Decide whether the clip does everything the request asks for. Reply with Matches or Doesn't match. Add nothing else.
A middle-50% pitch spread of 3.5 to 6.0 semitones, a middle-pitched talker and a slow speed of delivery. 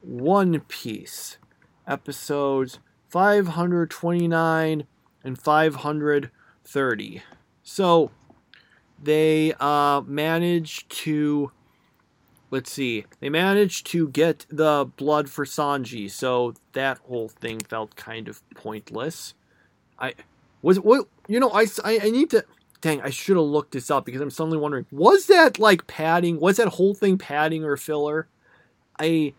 Matches